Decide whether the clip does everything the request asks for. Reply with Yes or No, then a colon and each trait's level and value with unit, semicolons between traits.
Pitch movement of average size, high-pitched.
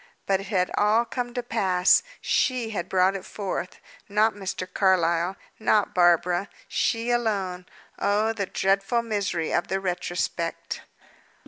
Yes: average, 3.2 semitones; high, 195 Hz